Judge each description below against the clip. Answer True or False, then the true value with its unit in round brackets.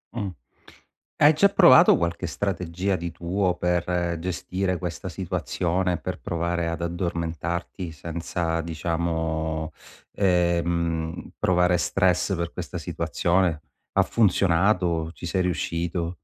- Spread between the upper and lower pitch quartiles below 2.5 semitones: True (1.6 semitones)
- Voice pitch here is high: False (85 Hz)